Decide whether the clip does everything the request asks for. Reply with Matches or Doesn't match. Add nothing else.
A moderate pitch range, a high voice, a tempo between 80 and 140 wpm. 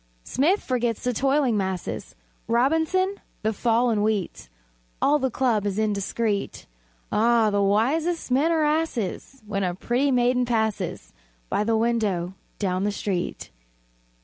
Matches